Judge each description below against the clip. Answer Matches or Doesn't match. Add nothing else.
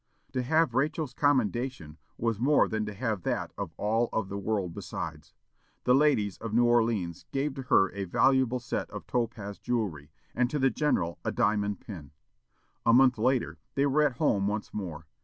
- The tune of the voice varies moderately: Matches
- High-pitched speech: Doesn't match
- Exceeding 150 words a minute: Matches